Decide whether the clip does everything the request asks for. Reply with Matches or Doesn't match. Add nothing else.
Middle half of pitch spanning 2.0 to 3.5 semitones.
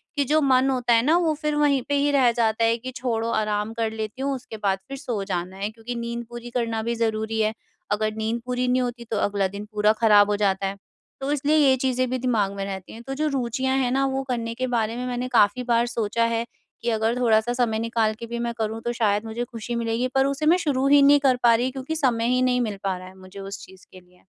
Matches